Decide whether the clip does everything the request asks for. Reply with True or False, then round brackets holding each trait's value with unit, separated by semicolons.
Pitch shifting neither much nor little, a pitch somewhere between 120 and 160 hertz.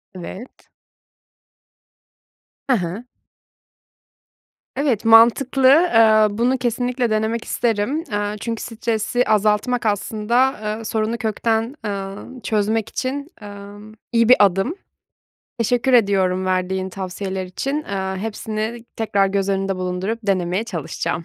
False (3.2 semitones; 215 Hz)